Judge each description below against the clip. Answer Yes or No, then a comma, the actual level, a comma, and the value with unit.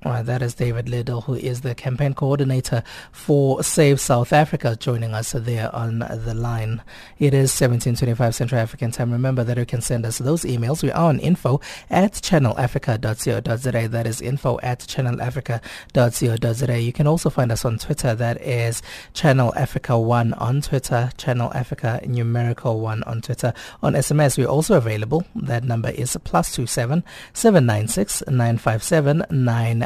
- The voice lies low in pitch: Yes, low, 125 Hz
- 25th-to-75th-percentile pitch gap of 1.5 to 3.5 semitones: Yes, average, 2.8 semitones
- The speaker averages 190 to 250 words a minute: No, average, 160 wpm